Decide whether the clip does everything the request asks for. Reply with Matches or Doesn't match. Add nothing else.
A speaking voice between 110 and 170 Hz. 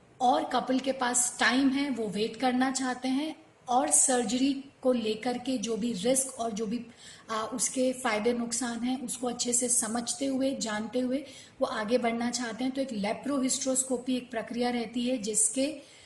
Doesn't match